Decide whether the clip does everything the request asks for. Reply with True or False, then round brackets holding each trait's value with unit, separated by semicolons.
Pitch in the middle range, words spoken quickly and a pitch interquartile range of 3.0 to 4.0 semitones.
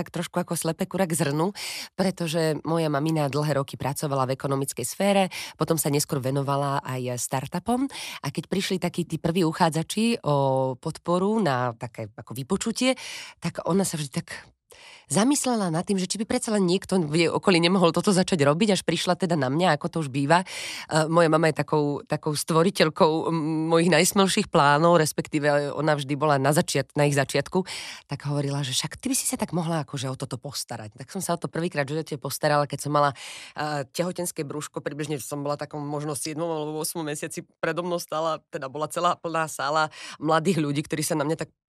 True (160 Hz; 195 wpm; 3.3 semitones)